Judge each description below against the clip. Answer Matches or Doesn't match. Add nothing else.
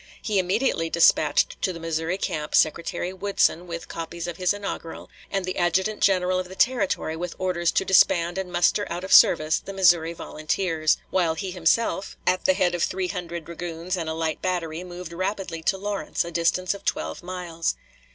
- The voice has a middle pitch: Matches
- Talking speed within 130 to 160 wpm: Doesn't match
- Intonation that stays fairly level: Matches